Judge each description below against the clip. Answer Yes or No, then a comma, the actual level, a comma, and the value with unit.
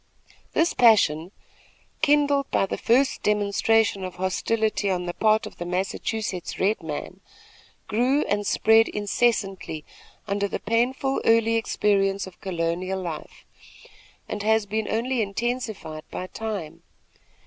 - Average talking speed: No, slow, 125 wpm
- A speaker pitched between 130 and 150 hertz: No, high, 205 Hz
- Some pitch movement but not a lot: Yes, average, 3.3 semitones